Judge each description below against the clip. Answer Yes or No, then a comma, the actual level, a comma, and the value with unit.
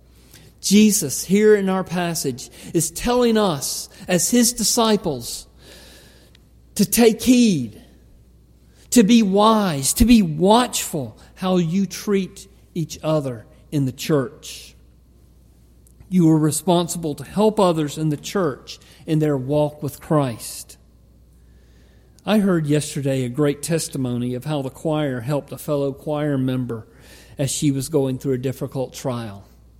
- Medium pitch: Yes, medium, 145 Hz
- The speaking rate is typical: No, slow, 130 wpm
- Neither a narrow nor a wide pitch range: No, wide, 7.0 semitones